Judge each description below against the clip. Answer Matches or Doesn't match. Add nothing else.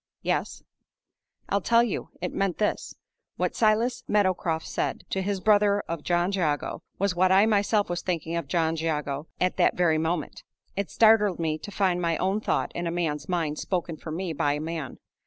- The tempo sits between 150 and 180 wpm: Doesn't match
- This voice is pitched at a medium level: Matches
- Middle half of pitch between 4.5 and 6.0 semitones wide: Doesn't match